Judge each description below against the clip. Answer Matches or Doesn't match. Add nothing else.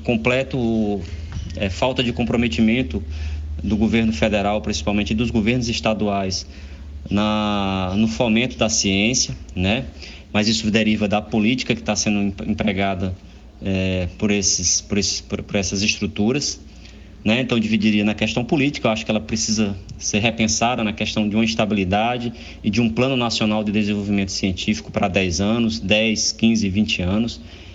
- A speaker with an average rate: Matches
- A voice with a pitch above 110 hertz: Doesn't match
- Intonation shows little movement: Matches